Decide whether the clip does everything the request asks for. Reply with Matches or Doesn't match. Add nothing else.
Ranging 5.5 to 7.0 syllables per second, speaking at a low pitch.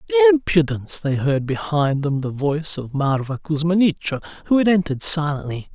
Doesn't match